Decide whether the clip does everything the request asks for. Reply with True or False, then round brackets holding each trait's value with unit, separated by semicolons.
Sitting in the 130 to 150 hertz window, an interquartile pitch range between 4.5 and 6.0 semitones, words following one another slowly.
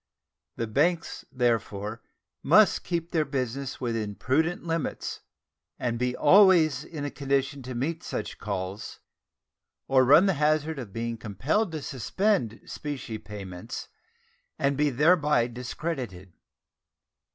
True (135 Hz; 5.3 semitones; 120 wpm)